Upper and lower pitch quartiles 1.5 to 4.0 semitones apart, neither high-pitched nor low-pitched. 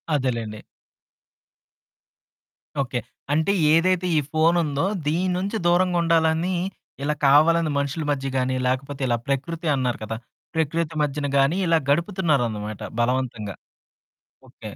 No: average, 4.4 semitones; medium, 150 Hz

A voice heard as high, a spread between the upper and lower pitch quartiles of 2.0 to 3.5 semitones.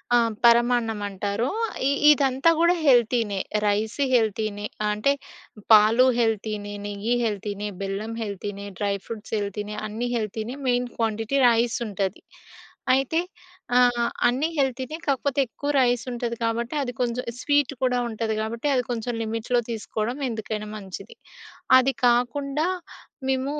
Yes: high, 230 Hz; average, 2.9 semitones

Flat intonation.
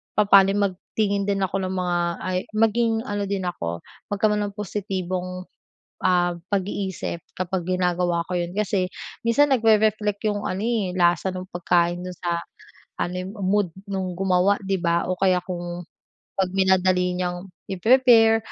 Yes: narrow, 2.3 semitones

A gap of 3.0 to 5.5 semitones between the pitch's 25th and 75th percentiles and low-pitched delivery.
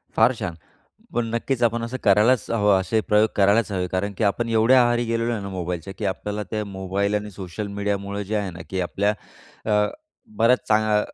No: narrow, 2.6 semitones; low, 105 Hz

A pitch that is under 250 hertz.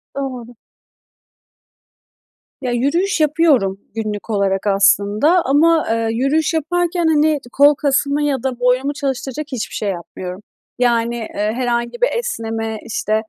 No: very high, 255 Hz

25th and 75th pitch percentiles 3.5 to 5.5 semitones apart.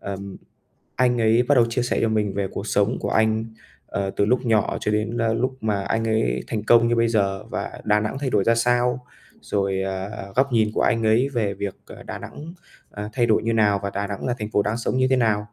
No: average, 2.7 semitones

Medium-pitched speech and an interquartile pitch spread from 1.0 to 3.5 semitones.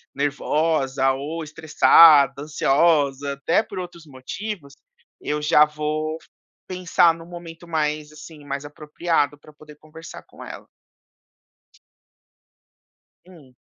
Yes: medium, 150 Hz; narrow, 2.4 semitones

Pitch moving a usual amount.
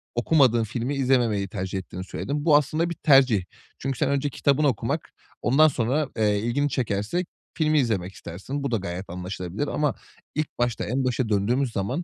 No: wide, 5.8 semitones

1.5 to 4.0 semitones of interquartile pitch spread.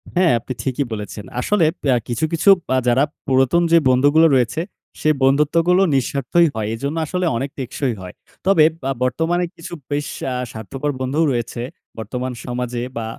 No: average, 4.7 semitones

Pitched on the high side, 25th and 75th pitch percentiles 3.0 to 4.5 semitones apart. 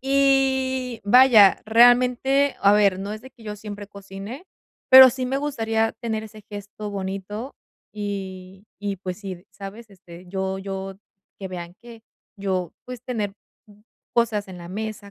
Yes: high, 210 Hz; average, 3.9 semitones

